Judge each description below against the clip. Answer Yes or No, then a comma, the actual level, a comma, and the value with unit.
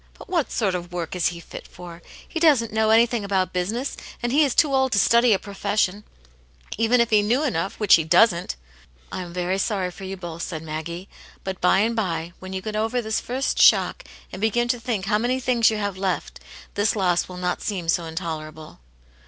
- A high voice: Yes, high, 200 Hz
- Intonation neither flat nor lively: Yes, average, 4.5 semitones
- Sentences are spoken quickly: Yes, fast, 220 wpm